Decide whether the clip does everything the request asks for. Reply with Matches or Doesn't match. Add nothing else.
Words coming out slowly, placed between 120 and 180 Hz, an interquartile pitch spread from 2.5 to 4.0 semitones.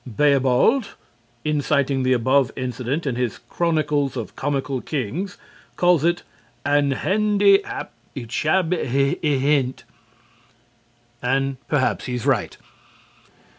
Matches